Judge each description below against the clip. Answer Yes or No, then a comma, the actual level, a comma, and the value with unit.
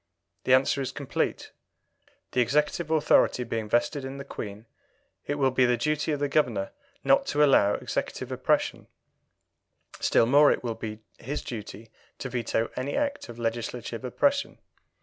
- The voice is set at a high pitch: No, low, 130 Hz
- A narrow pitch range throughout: No, average, 4.1 semitones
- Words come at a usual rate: Yes, average, 155 wpm